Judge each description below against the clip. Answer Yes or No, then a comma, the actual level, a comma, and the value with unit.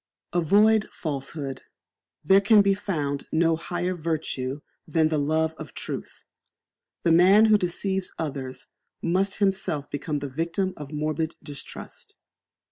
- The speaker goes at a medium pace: No, slow, 125 wpm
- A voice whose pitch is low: No, medium, 165 Hz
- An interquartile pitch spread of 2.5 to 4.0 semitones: No, average, 4.5 semitones